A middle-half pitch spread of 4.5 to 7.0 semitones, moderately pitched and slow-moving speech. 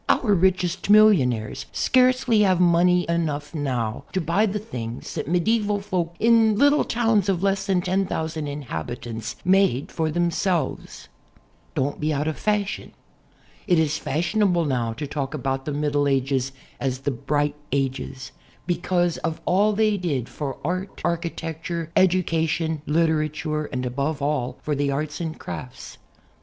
No: average, 5.0 semitones; medium, 160 Hz; average, 145 wpm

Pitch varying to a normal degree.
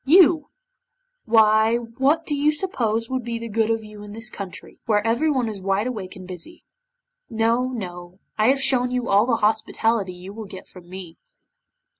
Yes: average, 3.8 semitones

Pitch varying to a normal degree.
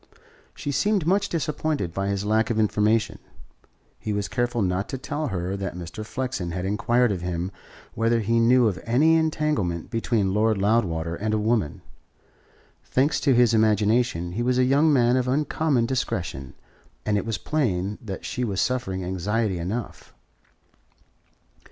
Yes: average, 4.7 semitones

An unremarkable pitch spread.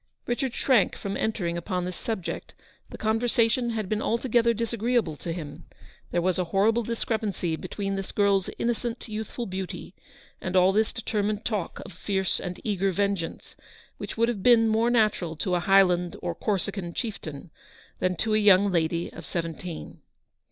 Yes: average, 3.8 semitones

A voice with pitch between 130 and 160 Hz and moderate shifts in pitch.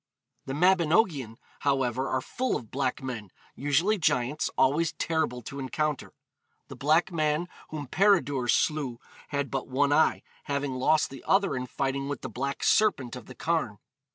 Yes: medium, 140 Hz; average, 3.5 semitones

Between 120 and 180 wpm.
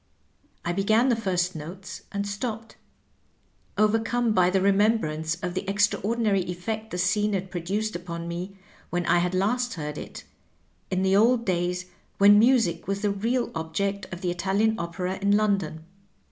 Yes: average, 160 wpm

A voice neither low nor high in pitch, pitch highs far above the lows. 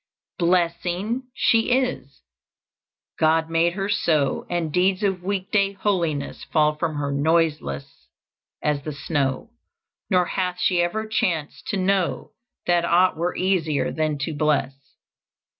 No: medium, 170 Hz; average, 3.8 semitones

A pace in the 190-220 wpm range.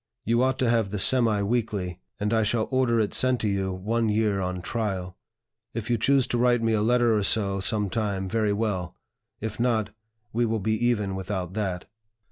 Yes: average, 200 wpm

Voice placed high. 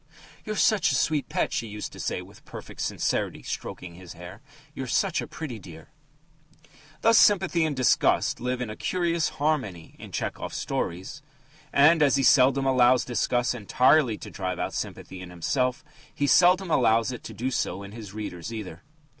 No: low, 125 Hz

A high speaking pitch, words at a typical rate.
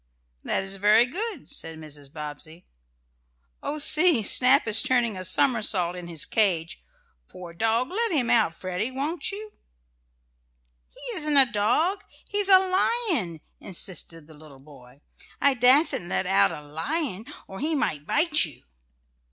Yes: high, 215 Hz; average, 145 wpm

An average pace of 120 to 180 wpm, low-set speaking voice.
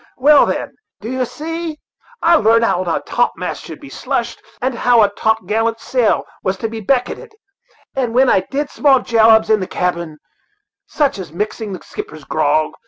No: average, 170 wpm; high, 230 Hz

